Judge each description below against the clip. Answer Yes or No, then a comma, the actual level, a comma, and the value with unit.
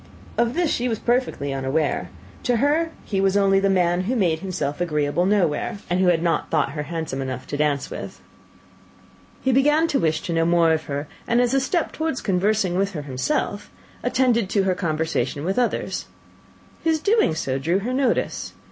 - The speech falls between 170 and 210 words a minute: Yes, average, 190 wpm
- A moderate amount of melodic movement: No, wide, 7.3 semitones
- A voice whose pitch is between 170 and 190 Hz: Yes, medium, 185 Hz